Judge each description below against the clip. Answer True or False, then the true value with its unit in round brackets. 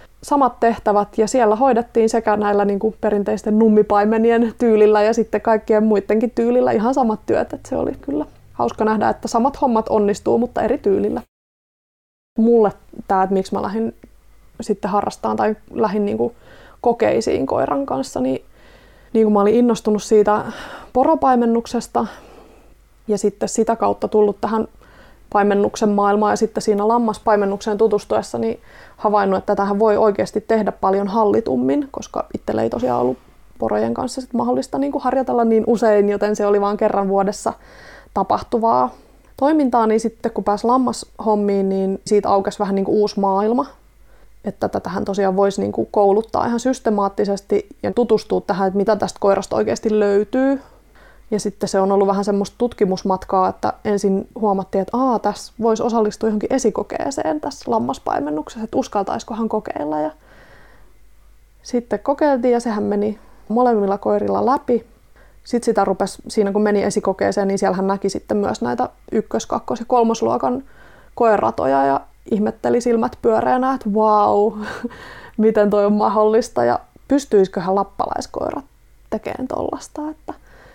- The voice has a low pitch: False (215 Hz)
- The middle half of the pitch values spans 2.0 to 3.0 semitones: True (2.6 semitones)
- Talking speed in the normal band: True (145 wpm)